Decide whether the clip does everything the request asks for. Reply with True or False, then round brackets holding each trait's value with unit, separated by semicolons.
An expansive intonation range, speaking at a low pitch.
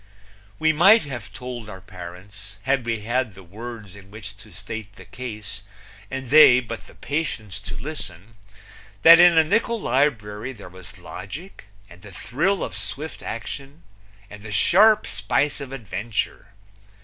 True (5.7 semitones; 115 Hz)